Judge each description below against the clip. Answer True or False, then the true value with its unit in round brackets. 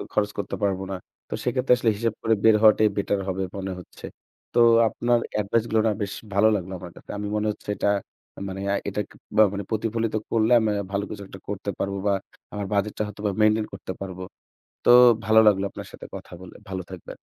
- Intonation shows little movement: True (2.0 semitones)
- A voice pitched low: True (105 Hz)